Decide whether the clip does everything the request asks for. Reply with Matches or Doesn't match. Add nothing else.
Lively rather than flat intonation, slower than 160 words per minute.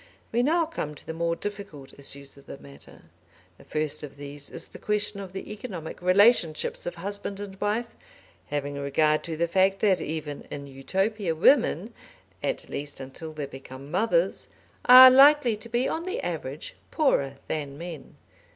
Doesn't match